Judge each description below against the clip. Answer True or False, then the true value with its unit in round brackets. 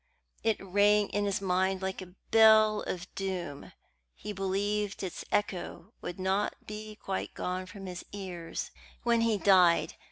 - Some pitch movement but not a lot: False (2.2 semitones)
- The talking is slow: False (150 wpm)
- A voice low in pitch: False (195 Hz)